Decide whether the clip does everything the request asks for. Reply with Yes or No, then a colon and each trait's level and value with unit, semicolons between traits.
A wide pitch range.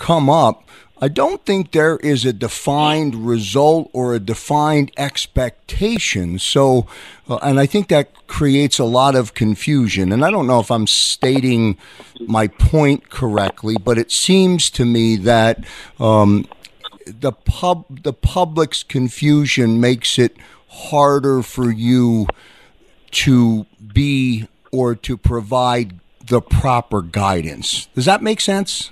No: average, 4.2 semitones